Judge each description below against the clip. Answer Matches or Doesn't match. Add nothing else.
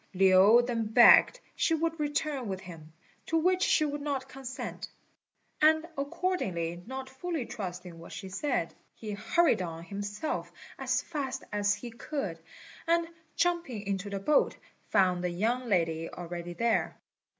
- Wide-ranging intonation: Matches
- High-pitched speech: Matches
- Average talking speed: Matches